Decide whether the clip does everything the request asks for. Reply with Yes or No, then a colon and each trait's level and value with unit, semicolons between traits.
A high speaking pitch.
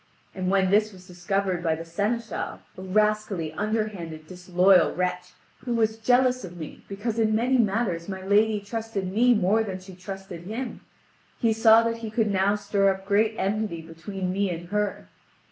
Yes: high, 200 Hz